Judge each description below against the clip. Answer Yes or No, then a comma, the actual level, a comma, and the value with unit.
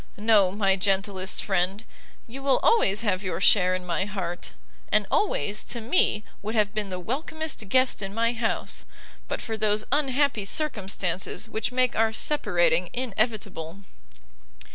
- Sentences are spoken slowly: No, average, 145 wpm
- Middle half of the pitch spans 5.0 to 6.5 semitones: No, average, 3.7 semitones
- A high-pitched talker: Yes, high, 210 Hz